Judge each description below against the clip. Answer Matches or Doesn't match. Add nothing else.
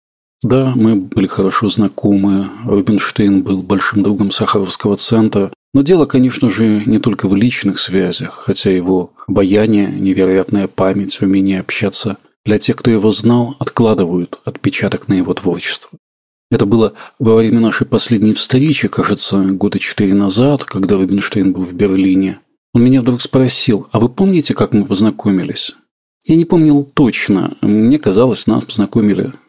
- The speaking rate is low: Doesn't match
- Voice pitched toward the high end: Doesn't match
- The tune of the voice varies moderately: Matches